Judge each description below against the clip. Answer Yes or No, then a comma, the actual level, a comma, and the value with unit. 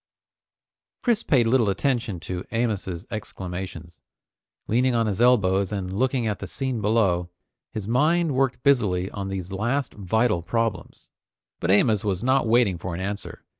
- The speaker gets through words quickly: No, average, 150 wpm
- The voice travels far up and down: No, average, 4.6 semitones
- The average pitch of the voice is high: No, low, 105 Hz